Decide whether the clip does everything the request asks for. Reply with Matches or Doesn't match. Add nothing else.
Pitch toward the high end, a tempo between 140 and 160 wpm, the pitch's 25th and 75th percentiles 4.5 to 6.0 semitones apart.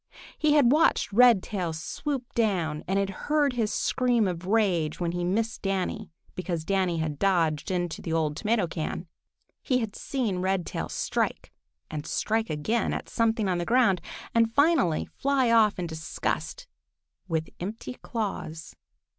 Matches